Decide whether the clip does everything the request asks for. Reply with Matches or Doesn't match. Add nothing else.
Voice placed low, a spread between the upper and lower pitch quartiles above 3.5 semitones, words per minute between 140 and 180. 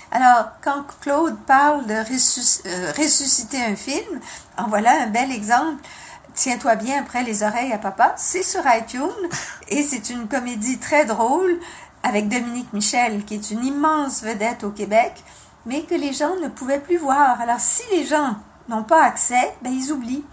Doesn't match